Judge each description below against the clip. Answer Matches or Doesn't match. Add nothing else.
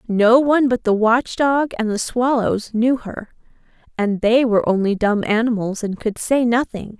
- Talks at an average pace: Matches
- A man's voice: Doesn't match